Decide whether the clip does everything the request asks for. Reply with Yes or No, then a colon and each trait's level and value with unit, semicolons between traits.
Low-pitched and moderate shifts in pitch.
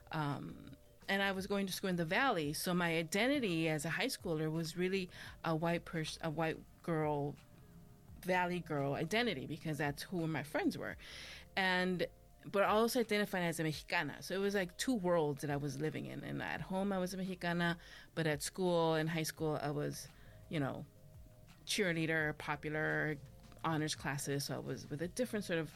No: medium, 165 Hz; average, 3.6 semitones